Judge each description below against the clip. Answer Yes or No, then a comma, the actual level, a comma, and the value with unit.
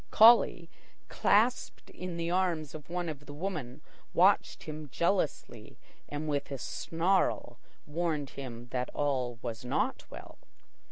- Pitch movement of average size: Yes, average, 4.2 semitones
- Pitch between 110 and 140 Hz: No, medium, 155 Hz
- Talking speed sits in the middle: No, slow, 130 wpm